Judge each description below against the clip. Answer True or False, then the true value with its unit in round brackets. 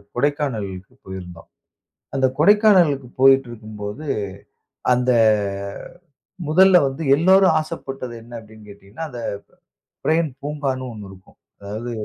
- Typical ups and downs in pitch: False (6.2 semitones)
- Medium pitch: False (130 Hz)